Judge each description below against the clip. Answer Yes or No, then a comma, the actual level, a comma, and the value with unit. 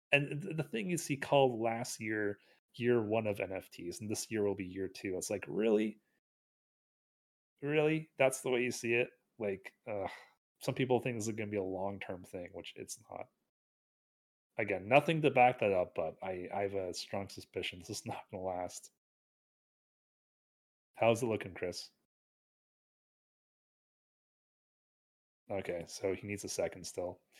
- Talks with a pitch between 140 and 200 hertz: No, low, 115 Hz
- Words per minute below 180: Yes, average, 165 wpm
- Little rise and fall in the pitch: No, average, 5.1 semitones